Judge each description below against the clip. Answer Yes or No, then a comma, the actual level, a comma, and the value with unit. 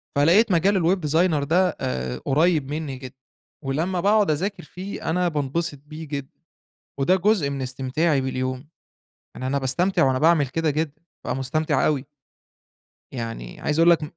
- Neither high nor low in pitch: Yes, medium, 150 Hz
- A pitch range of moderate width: Yes, average, 4.3 semitones